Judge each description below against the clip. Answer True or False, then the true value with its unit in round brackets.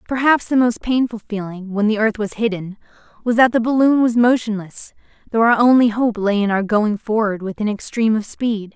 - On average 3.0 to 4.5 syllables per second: False (5.3 syllables/s)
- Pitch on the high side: True (220 Hz)